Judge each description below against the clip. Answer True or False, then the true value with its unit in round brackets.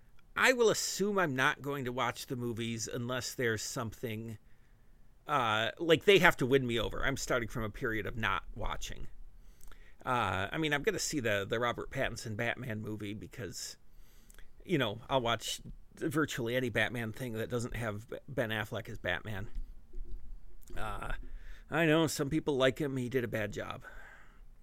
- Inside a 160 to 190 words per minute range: True (170 wpm)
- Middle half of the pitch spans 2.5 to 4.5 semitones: True (3.7 semitones)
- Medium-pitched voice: False (120 Hz)